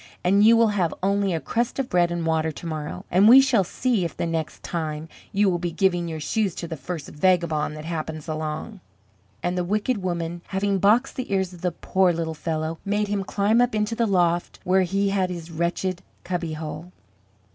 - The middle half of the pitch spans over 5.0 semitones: No, average, 3.5 semitones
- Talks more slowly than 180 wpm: No, fast, 205 wpm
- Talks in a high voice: No, medium, 180 Hz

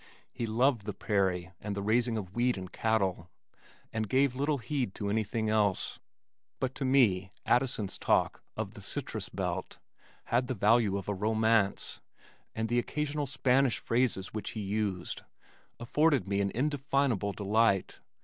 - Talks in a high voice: No, low, 110 Hz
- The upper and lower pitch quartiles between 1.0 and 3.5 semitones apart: No, average, 4.0 semitones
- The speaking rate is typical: Yes, average, 150 wpm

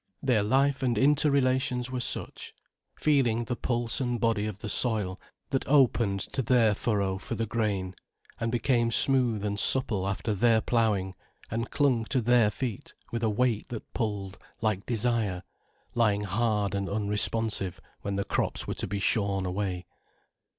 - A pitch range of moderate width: Yes, average, 3.3 semitones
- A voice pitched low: Yes, low, 115 Hz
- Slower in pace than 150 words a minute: No, average, 155 wpm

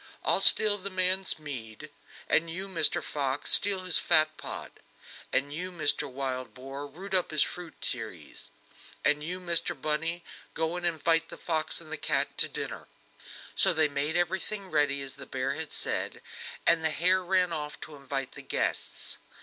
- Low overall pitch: No, medium, 160 Hz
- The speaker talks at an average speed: Yes, average, 170 wpm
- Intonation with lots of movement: No, average, 3.8 semitones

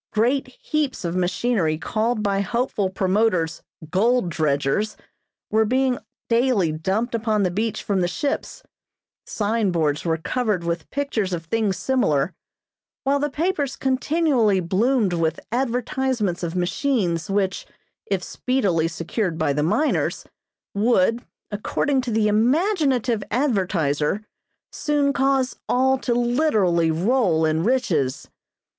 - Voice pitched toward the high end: Yes, high, 215 Hz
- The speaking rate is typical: No, slow, 120 wpm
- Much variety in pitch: Yes, wide, 6.5 semitones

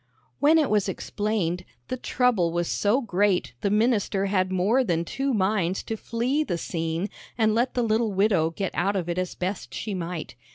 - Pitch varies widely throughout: No, average, 4.1 semitones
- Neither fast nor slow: Yes, average, 190 wpm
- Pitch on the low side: No, high, 200 Hz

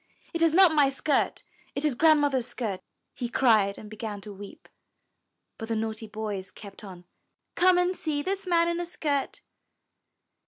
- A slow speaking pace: No, average, 170 wpm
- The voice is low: No, very high, 260 Hz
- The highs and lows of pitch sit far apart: Yes, wide, 7.2 semitones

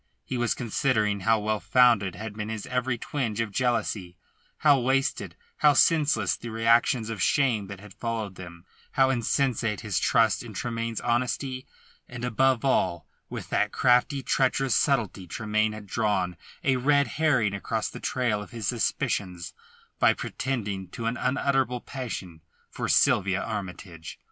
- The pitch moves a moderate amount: Yes, average, 3.9 semitones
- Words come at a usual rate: Yes, average, 150 wpm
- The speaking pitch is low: Yes, low, 115 Hz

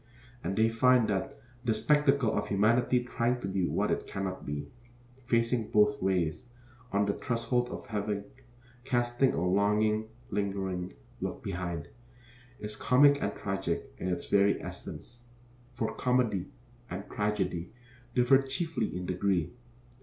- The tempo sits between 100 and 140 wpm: Yes, slow, 135 wpm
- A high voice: No, low, 105 Hz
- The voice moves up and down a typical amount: Yes, average, 4.2 semitones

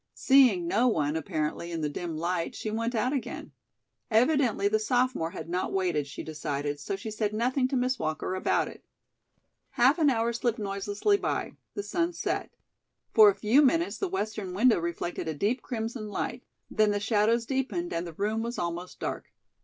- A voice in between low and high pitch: No, high, 215 Hz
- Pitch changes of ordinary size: No, wide, 6.4 semitones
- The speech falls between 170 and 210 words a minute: Yes, average, 185 wpm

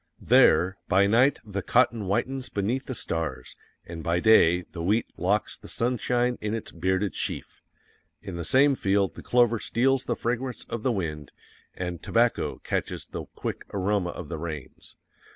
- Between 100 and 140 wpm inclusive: No, average, 165 wpm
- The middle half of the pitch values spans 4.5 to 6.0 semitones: Yes, wide, 5.5 semitones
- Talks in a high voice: No, low, 100 Hz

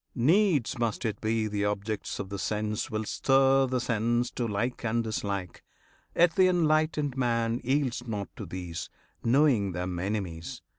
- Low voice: Yes, low, 115 Hz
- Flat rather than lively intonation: No, average, 4.5 semitones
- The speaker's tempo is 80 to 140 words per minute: No, average, 155 wpm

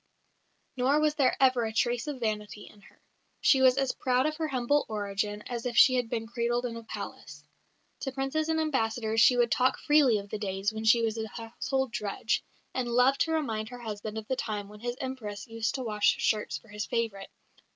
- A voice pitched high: Yes, high, 235 Hz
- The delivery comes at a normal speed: No, fast, 215 wpm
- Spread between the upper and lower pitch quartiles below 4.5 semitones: Yes, average, 3.2 semitones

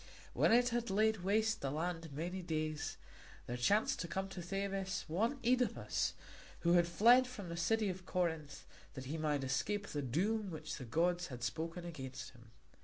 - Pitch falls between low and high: Yes, medium, 175 Hz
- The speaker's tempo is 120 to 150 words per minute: No, average, 180 wpm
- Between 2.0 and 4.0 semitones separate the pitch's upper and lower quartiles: No, average, 4.8 semitones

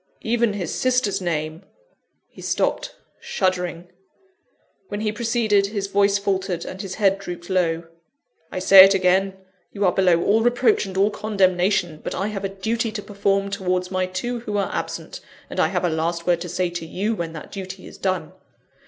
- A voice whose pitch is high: Yes, high, 195 Hz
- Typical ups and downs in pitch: No, narrow, 2.3 semitones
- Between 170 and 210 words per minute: Yes, average, 190 wpm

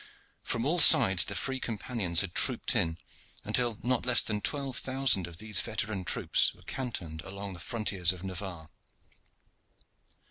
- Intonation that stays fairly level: No, average, 5.2 semitones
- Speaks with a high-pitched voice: No, low, 105 Hz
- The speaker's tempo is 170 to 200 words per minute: No, average, 150 wpm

